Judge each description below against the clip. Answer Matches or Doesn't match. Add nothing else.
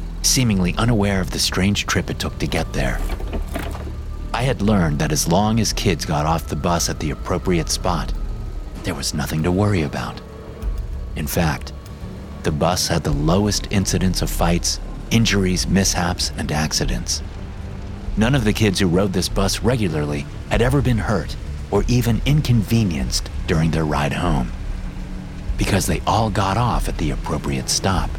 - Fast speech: Doesn't match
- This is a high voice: Doesn't match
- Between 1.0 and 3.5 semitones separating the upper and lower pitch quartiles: Doesn't match